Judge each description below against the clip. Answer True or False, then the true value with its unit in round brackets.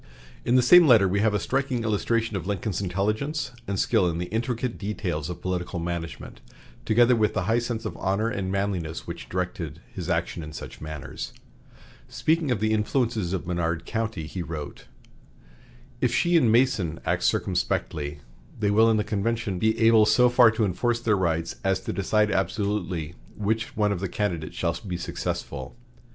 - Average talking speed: True (175 wpm)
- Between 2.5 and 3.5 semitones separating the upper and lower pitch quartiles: False (4.5 semitones)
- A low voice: True (105 Hz)